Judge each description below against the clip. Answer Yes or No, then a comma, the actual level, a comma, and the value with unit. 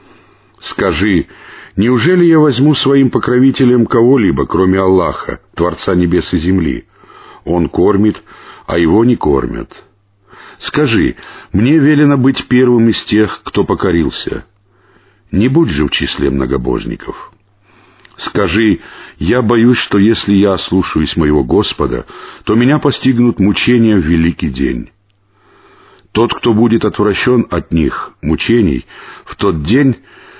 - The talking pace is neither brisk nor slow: Yes, average, 120 wpm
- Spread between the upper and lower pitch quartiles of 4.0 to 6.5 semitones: Yes, average, 4.7 semitones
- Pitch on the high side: No, low, 110 Hz